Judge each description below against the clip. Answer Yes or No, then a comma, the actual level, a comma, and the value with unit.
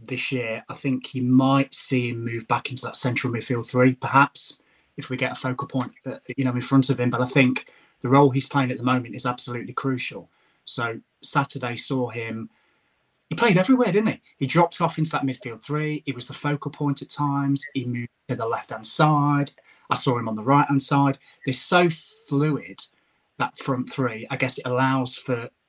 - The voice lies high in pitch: No, low, 135 Hz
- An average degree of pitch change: No, narrow, 2.2 semitones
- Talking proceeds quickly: Yes, fast, 215 wpm